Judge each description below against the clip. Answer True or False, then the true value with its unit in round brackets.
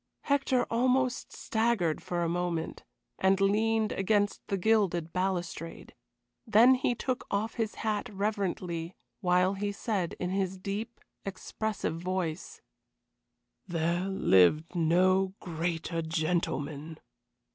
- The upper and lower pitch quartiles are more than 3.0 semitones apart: True (4.0 semitones)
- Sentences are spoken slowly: True (110 wpm)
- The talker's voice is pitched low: False (190 Hz)